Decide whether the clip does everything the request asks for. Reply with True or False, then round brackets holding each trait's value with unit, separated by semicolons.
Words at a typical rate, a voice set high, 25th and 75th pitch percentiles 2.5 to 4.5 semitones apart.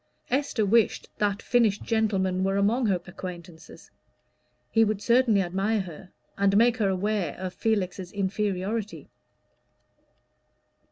False (115 wpm; 200 Hz; 2.9 semitones)